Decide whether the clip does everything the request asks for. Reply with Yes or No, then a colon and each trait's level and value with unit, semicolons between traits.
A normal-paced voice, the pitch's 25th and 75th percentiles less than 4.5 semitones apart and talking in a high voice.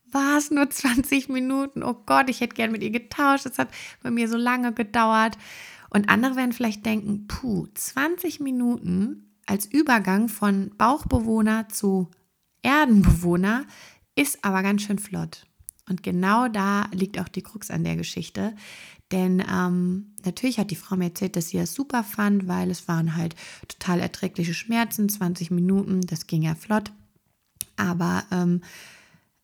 No: average, 160 wpm; average, 4.8 semitones; high, 205 Hz